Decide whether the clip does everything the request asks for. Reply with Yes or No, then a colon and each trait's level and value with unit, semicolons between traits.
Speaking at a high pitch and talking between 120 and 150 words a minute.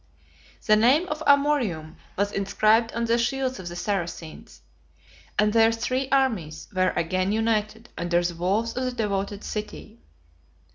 Yes: high, 215 Hz; average, 145 wpm